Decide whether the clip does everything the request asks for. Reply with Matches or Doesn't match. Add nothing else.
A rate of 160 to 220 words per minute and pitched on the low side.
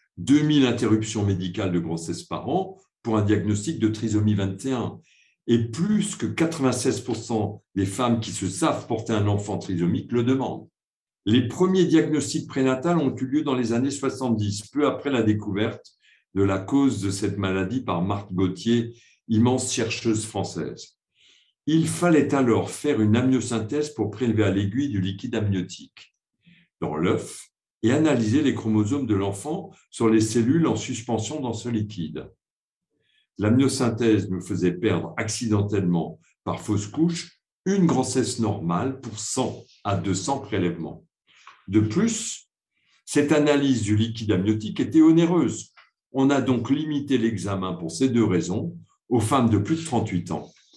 Doesn't match